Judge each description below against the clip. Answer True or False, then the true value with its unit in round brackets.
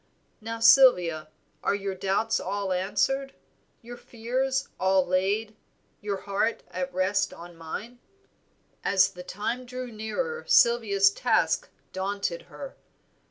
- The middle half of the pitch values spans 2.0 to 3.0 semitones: False (4.2 semitones)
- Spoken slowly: True (115 wpm)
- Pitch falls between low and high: False (205 Hz)